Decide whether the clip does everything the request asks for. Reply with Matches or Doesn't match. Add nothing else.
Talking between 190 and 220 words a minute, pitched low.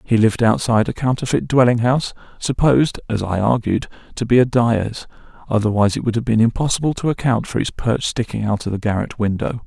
Matches